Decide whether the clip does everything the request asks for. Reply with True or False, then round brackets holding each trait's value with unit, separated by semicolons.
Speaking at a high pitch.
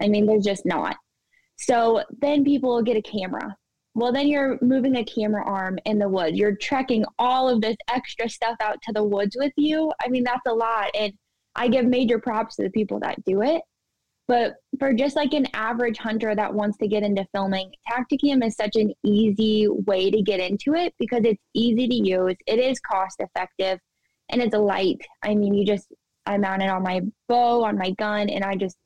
True (220 Hz)